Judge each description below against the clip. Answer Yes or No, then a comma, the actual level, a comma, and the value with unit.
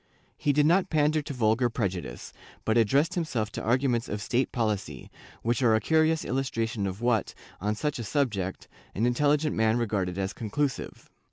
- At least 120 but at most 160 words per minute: No, average, 170 wpm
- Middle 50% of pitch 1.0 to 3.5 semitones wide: No, average, 5.2 semitones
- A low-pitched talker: Yes, low, 120 Hz